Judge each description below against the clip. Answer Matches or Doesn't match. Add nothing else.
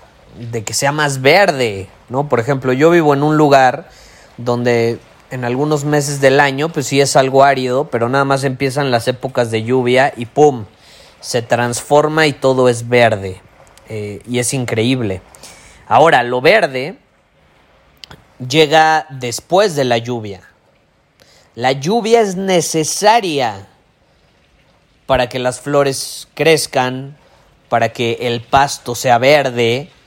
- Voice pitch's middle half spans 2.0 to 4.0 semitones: Matches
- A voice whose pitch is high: Doesn't match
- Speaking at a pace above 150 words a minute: Doesn't match